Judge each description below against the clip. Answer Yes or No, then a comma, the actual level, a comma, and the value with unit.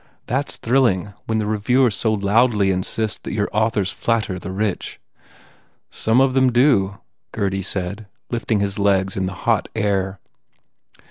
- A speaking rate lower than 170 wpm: Yes, average, 150 wpm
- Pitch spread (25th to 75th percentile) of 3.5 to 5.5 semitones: No, average, 3.0 semitones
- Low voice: Yes, low, 105 Hz